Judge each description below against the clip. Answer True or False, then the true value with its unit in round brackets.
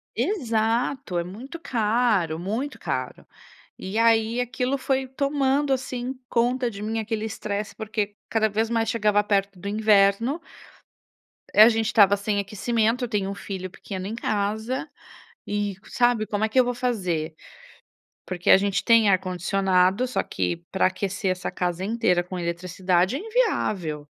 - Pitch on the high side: True (215 Hz)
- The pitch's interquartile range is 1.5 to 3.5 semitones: False (3.9 semitones)